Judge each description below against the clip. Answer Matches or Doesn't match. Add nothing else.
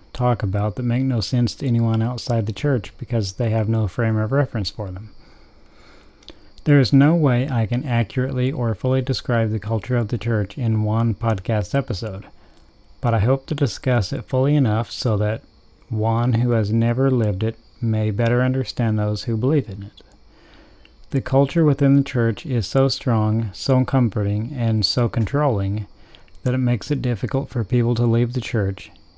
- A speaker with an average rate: Matches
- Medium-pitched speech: Doesn't match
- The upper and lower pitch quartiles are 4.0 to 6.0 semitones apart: Doesn't match